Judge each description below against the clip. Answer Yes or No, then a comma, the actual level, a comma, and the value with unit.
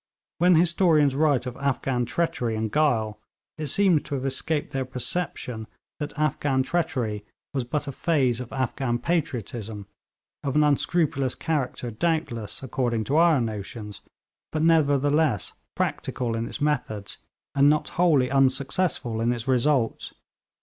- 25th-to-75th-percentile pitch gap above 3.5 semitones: Yes, average, 4.3 semitones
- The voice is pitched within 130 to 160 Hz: Yes, low, 135 Hz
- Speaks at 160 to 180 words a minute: No, slow, 135 wpm